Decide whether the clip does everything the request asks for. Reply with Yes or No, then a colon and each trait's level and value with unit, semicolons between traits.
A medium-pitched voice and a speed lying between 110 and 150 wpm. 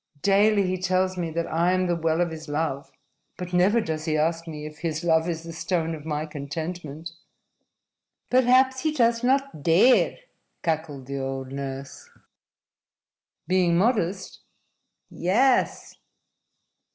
Yes: medium, 170 Hz; average, 140 wpm